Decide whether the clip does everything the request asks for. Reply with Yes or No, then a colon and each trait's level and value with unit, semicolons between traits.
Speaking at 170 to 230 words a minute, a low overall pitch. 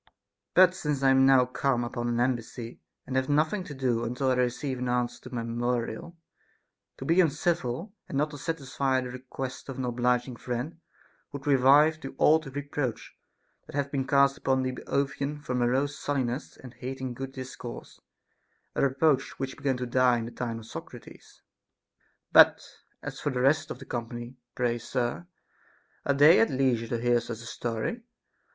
Yes: average, 180 wpm; low, 130 Hz